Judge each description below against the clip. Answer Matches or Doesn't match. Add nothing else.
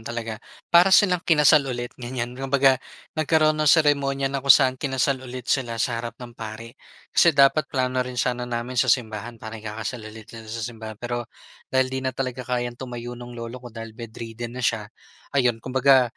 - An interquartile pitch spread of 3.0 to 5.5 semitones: Doesn't match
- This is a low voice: Matches